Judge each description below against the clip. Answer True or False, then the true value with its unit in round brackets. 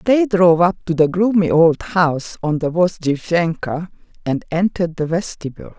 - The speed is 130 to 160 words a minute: True (155 wpm)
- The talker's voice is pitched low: False (170 Hz)